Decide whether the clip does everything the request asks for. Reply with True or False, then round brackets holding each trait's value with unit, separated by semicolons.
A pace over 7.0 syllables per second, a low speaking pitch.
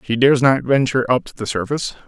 True (7.3 syllables/s; 130 Hz)